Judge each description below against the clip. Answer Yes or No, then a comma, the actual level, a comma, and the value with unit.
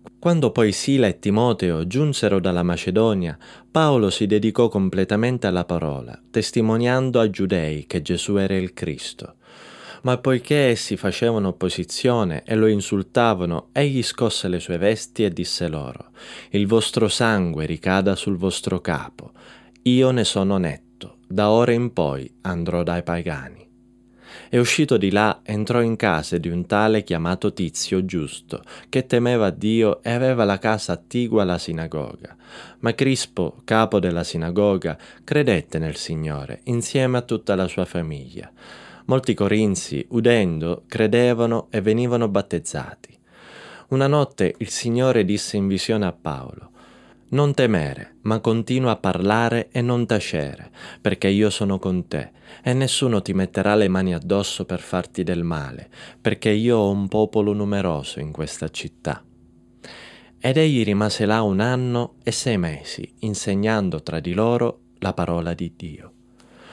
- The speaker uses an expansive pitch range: No, average, 4.9 semitones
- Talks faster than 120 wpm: Yes, average, 145 wpm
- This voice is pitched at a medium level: No, low, 105 Hz